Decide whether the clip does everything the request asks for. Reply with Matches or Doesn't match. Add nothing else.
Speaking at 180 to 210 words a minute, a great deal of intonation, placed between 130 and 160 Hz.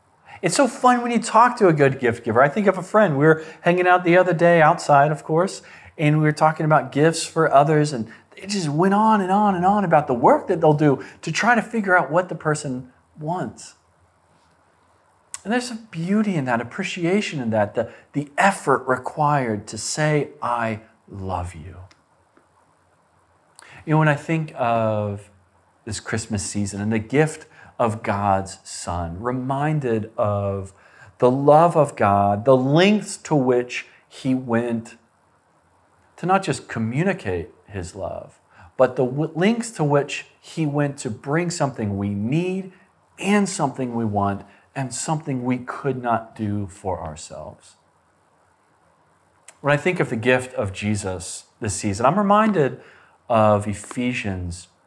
Doesn't match